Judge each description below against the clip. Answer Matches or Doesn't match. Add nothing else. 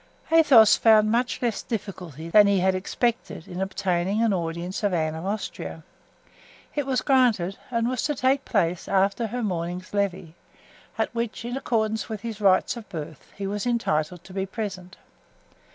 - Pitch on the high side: Matches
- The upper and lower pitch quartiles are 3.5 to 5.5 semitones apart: Matches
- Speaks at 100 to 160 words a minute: Doesn't match